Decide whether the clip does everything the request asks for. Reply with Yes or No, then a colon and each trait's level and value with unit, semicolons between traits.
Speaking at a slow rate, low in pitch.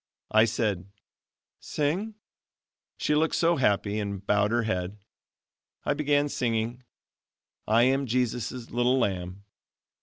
Yes: slow, 115 wpm; low, 115 Hz